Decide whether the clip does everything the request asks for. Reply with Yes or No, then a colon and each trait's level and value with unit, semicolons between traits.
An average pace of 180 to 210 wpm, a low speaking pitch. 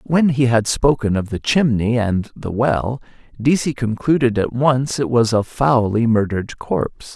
No: average, 170 wpm; low, 120 Hz